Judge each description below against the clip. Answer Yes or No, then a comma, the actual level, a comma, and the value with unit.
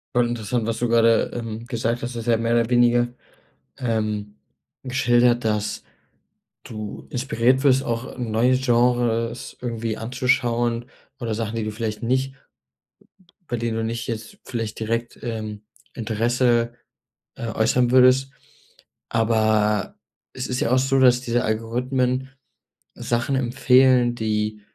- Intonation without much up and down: Yes, narrow, 1.8 semitones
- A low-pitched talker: Yes, low, 120 Hz